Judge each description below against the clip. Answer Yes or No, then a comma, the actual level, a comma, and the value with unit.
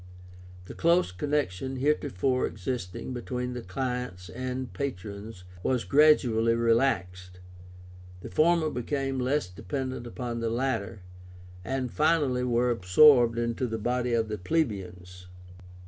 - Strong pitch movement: No, average, 4.0 semitones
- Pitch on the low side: Yes, low, 125 Hz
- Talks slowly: Yes, slow, 115 wpm